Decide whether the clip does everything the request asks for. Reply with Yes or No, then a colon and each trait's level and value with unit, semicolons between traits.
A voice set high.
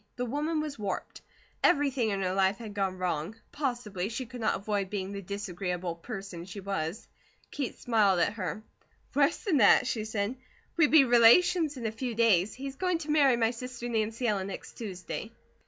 Yes: high, 220 Hz